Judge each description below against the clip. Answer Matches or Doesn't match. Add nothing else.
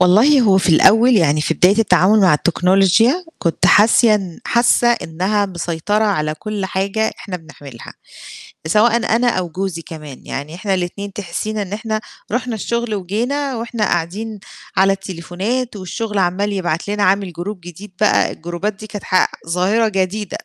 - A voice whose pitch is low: Doesn't match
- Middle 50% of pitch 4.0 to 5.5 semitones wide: Doesn't match